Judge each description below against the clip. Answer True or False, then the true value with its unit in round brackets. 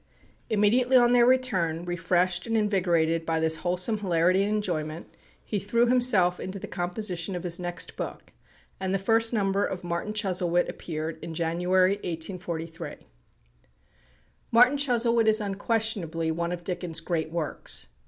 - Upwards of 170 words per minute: False (145 wpm)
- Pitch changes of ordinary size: True (4.0 semitones)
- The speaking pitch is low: False (185 Hz)